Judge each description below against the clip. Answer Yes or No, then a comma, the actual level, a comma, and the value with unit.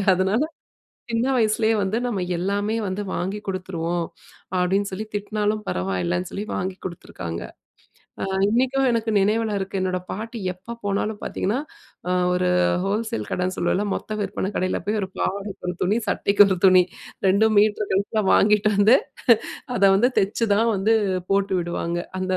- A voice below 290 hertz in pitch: Yes, high, 200 Hz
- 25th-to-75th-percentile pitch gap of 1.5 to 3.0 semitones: Yes, narrow, 2.6 semitones